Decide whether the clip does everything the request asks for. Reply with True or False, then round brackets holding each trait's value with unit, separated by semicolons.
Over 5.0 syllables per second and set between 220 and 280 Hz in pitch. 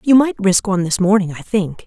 False (5.7 syllables/s; 200 Hz)